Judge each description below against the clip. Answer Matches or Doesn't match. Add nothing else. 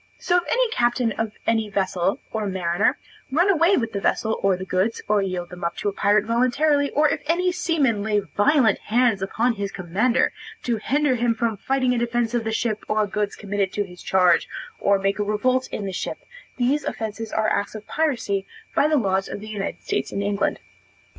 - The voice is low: Doesn't match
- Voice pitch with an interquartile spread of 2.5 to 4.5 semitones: Matches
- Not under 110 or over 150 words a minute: Doesn't match